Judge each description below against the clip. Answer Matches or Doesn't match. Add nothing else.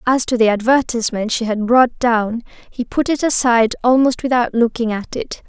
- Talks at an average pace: Matches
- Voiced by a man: Doesn't match